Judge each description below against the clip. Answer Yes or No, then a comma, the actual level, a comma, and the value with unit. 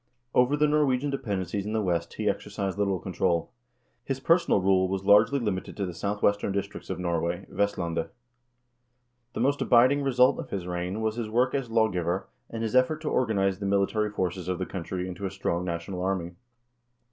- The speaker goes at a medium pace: Yes, average, 195 wpm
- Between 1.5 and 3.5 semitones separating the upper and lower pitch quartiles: No, average, 4.4 semitones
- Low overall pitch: Yes, low, 100 Hz